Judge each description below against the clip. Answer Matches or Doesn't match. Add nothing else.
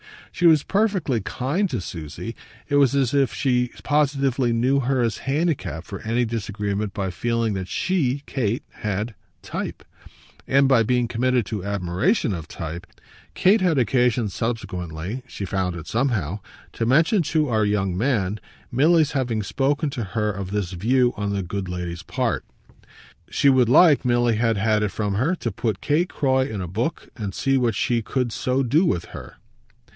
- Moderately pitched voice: Doesn't match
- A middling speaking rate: Matches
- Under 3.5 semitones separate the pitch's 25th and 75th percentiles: Doesn't match